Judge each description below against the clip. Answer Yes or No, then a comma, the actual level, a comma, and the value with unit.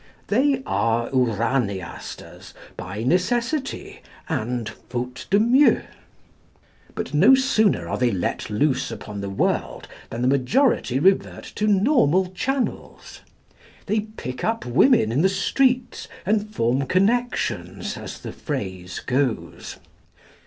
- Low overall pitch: No, medium, 165 Hz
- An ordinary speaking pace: No, slow, 115 wpm